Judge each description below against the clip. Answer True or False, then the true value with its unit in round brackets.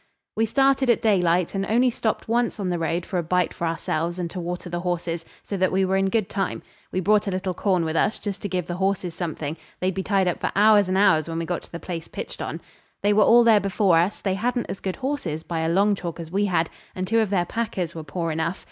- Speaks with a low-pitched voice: False (185 Hz)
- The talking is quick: True (265 wpm)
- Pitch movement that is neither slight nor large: True (3.3 semitones)